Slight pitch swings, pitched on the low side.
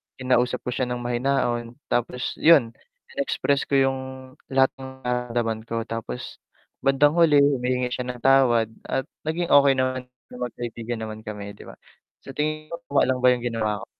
Yes: narrow, 2.3 semitones; low, 125 Hz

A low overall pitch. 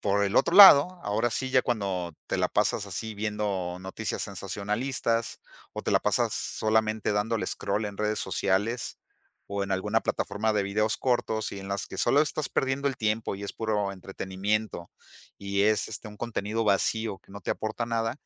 Yes: low, 105 Hz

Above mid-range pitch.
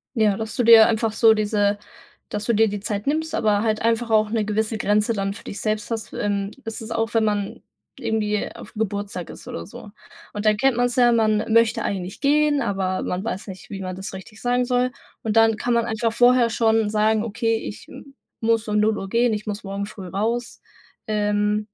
Yes: high, 215 Hz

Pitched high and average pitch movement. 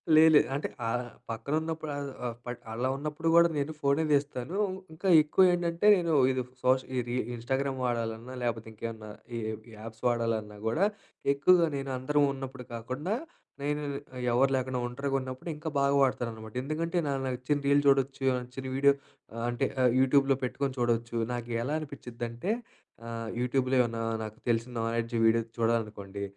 No: low, 130 Hz; average, 3.4 semitones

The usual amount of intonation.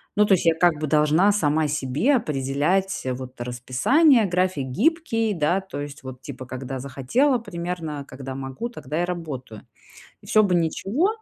No: wide, 6.5 semitones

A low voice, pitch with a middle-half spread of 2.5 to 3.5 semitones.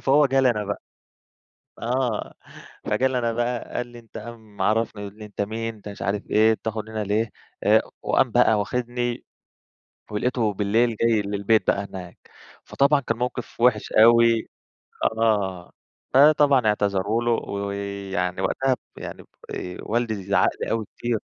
Yes: low, 110 Hz; average, 2.8 semitones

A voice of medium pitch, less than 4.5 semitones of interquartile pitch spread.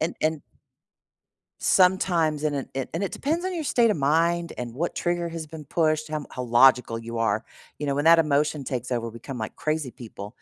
No: medium, 150 Hz; average, 4.9 semitones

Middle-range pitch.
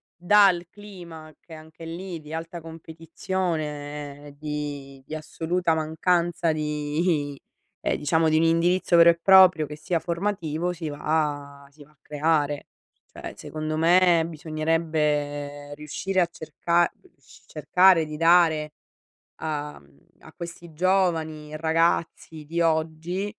Yes: medium, 160 Hz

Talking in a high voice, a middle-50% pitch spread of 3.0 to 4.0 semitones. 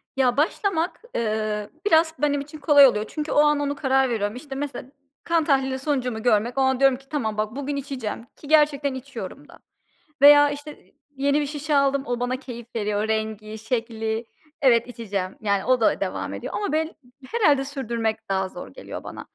No: very high, 265 Hz; average, 4.7 semitones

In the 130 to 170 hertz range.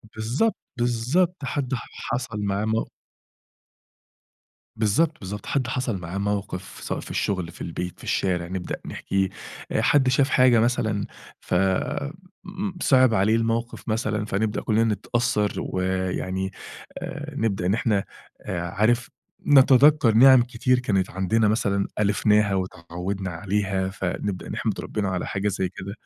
No: low, 105 Hz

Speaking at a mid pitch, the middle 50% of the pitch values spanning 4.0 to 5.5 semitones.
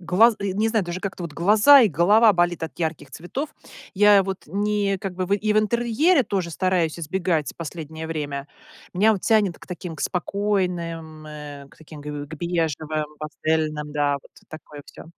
Yes: medium, 175 Hz; average, 4.6 semitones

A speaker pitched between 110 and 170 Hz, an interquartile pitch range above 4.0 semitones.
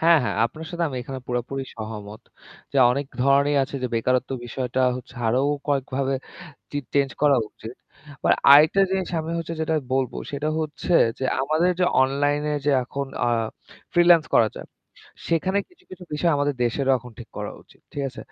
No: medium, 140 Hz; average, 3.7 semitones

